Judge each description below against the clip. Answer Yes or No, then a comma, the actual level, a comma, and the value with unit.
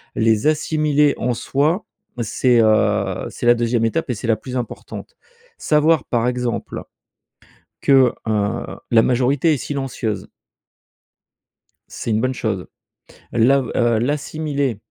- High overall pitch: No, low, 125 Hz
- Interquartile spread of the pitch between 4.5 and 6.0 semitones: No, average, 4.0 semitones